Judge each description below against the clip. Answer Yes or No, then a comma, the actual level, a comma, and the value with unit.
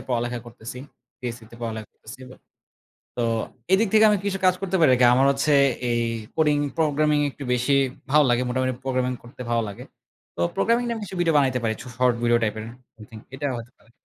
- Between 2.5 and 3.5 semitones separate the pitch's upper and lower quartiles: No, average, 4.4 semitones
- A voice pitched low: Yes, low, 130 Hz